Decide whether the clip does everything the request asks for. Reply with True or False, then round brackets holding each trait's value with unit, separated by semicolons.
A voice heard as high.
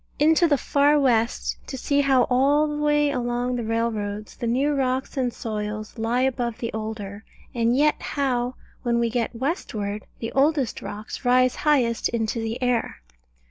True (245 Hz)